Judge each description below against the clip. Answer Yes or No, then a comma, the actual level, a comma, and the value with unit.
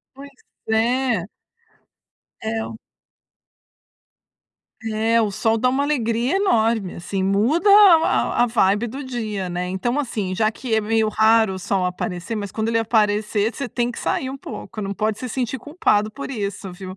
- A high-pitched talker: Yes, high, 220 Hz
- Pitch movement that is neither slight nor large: Yes, average, 3.3 semitones